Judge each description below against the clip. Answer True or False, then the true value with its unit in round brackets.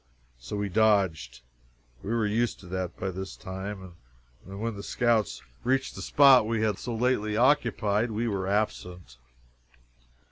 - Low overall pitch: True (105 Hz)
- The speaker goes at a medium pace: True (150 wpm)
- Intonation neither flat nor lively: True (3.4 semitones)